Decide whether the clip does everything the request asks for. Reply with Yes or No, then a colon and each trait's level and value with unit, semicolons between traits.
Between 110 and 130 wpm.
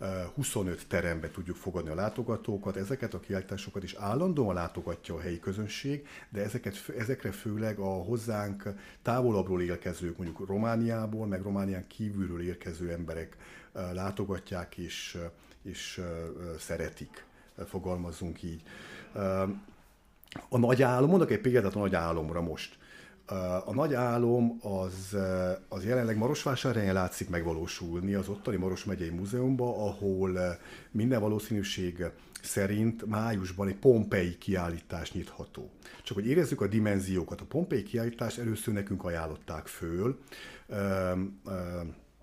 Yes: average, 115 wpm